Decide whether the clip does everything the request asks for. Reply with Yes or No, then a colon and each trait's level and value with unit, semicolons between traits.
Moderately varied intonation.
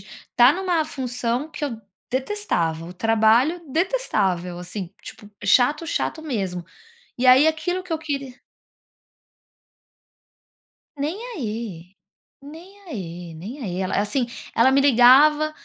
No: wide, 7.4 semitones